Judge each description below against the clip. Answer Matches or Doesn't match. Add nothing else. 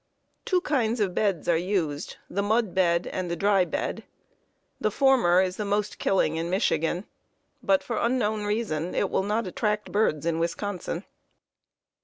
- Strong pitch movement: Doesn't match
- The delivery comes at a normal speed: Matches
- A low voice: Doesn't match